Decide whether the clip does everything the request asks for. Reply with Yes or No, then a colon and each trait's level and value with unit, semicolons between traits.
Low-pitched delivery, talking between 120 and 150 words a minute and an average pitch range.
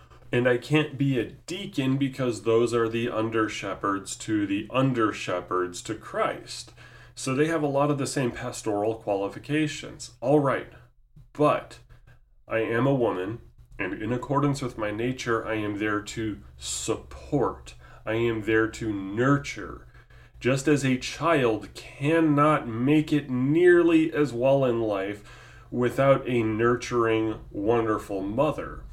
Yes: low, 120 Hz; average, 140 wpm; average, 4.1 semitones